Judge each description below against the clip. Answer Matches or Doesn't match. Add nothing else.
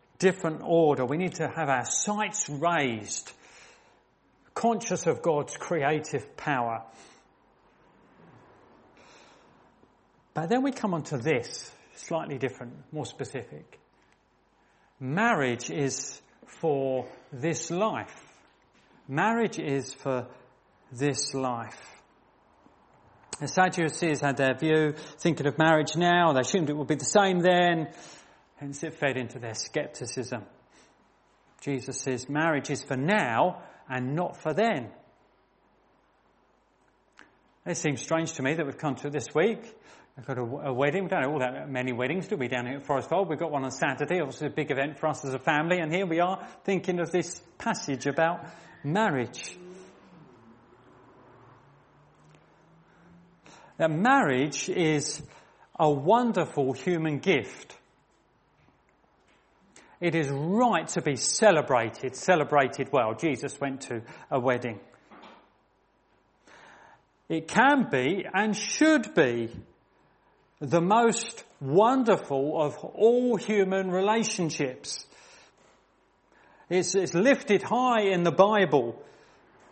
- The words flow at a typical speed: Doesn't match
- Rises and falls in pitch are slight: Doesn't match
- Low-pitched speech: Doesn't match